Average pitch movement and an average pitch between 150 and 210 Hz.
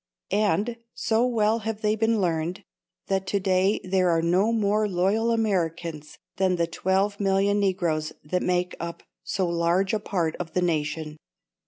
Yes: average, 3.5 semitones; high, 190 Hz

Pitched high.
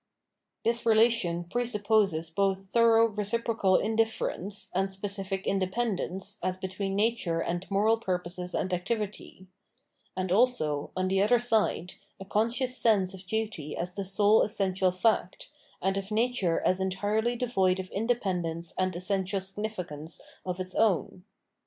Yes: high, 195 Hz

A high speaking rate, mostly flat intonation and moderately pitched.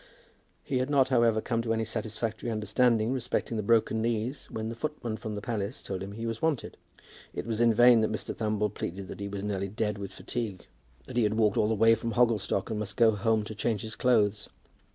No: fast, 225 wpm; narrow, 1.9 semitones; low, 110 Hz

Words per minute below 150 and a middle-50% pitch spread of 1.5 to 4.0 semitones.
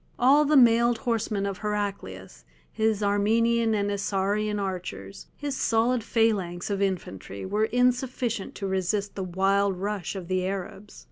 Yes: average, 140 wpm; average, 3.1 semitones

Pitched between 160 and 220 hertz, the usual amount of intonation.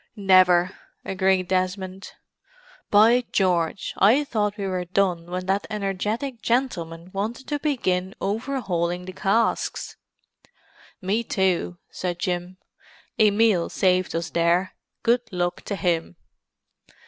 Yes: high, 190 Hz; average, 3.0 semitones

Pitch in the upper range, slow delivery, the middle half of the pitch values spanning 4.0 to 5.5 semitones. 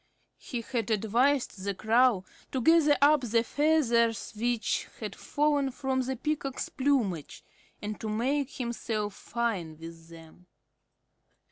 Yes: high, 235 Hz; slow, 125 wpm; average, 4.6 semitones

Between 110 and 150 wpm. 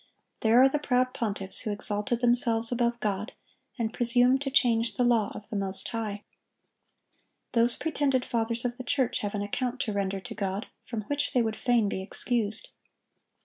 No: average, 180 wpm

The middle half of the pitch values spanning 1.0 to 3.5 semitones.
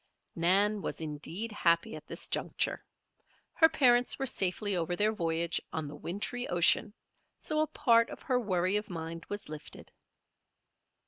No: wide, 5.4 semitones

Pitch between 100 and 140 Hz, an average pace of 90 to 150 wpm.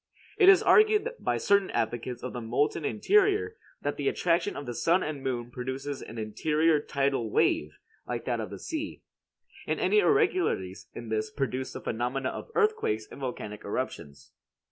No: low, 135 Hz; average, 165 wpm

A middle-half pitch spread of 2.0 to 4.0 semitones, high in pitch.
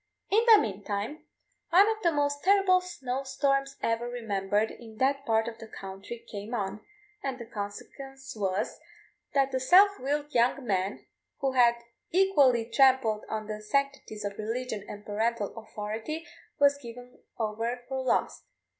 No: average, 4.4 semitones; high, 245 Hz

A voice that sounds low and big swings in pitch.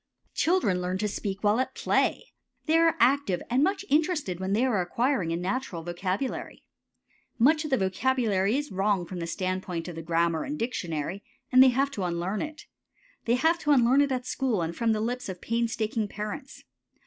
No: high, 220 Hz; wide, 6.3 semitones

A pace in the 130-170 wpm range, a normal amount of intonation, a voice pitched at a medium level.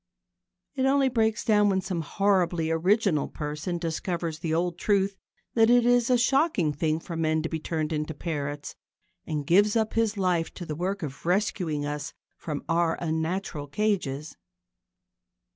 Yes: average, 160 wpm; average, 4.7 semitones; medium, 170 Hz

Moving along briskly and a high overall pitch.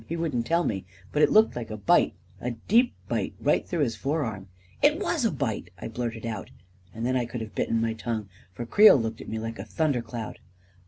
No: fast, 245 wpm; low, 115 Hz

